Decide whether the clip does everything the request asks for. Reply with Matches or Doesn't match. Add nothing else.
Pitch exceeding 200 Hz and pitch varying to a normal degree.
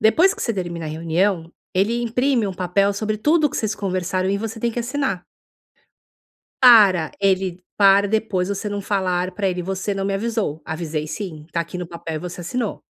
Doesn't match